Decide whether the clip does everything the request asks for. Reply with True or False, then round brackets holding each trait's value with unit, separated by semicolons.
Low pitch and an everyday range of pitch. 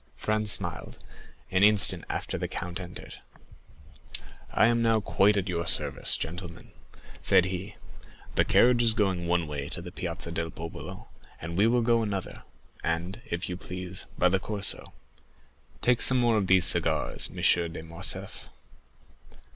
True (95 Hz; 3.8 semitones)